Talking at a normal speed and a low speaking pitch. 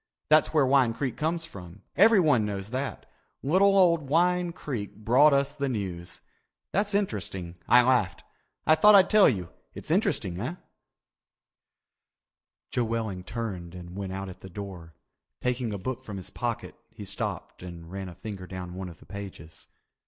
Yes: average, 160 wpm; low, 110 Hz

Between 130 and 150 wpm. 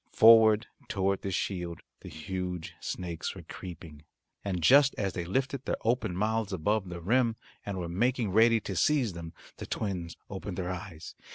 No: average, 170 wpm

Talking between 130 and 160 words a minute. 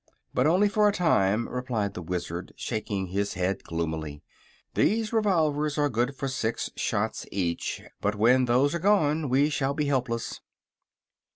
Yes: average, 155 wpm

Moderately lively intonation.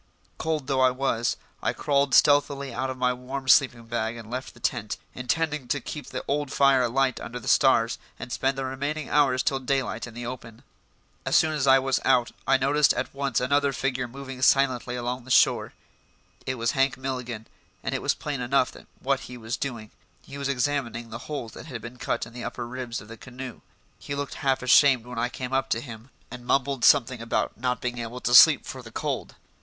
No: narrow, 2.2 semitones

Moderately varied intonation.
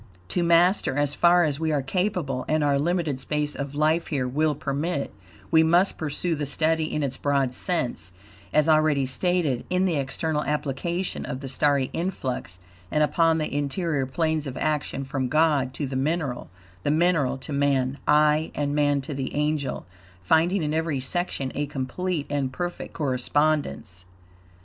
Yes: average, 3.0 semitones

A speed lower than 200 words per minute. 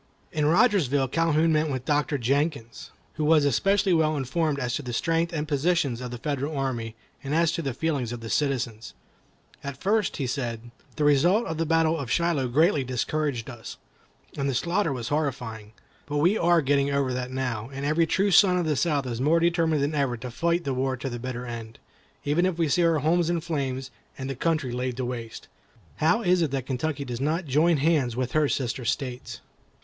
No: fast, 205 wpm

